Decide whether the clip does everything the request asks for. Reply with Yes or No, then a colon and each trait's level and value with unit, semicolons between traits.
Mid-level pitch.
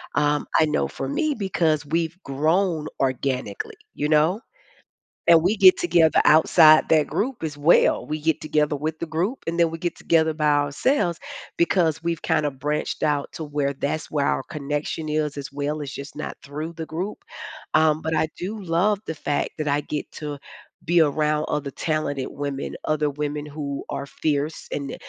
Yes: medium, 155 Hz